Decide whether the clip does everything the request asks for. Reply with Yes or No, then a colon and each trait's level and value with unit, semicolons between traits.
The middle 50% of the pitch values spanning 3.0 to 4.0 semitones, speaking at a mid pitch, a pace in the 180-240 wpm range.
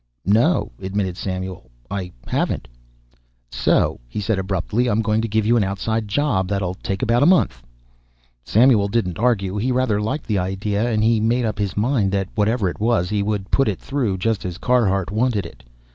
No: average, 3.3 semitones; low, 105 Hz; average, 190 wpm